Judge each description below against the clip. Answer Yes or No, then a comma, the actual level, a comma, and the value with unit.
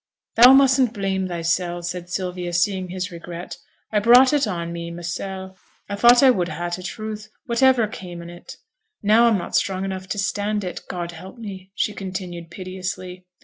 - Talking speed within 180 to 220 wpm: Yes, average, 185 wpm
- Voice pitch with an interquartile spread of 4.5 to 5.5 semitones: No, average, 3.4 semitones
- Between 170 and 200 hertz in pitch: Yes, high, 190 Hz